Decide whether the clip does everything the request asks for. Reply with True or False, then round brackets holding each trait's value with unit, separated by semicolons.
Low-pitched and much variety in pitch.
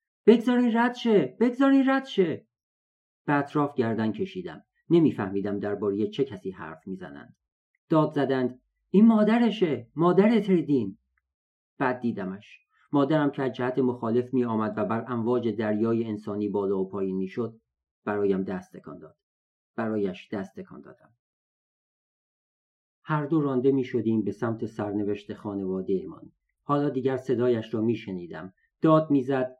True (120 Hz; 6.1 semitones)